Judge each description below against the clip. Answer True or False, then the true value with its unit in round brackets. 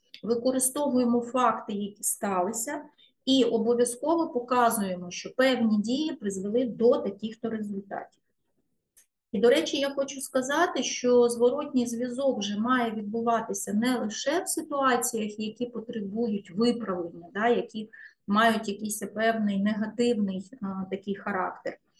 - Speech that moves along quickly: False (115 wpm)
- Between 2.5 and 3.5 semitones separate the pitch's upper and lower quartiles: True (3.1 semitones)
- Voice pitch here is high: True (235 Hz)